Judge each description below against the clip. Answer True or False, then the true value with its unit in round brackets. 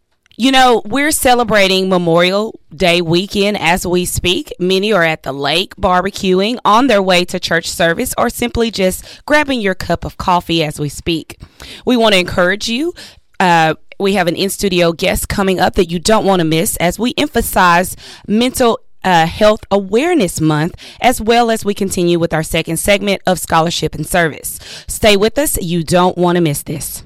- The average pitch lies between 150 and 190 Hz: True (185 Hz)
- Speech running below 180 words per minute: False (185 wpm)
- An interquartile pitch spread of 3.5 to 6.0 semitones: True (4.1 semitones)